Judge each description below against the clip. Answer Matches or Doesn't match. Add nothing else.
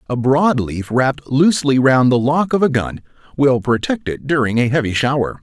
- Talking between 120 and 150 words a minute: Doesn't match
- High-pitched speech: Doesn't match